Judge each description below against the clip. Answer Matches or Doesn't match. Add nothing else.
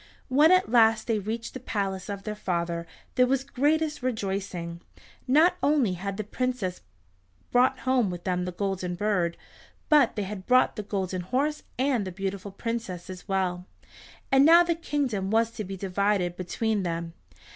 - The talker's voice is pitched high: Matches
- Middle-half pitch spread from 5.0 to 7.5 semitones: Matches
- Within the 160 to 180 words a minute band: Matches